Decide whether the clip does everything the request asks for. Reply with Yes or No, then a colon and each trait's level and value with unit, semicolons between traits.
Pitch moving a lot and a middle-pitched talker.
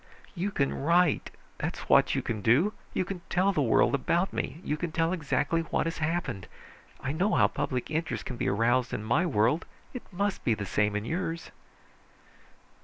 Yes: wide, 6.5 semitones; medium, 155 Hz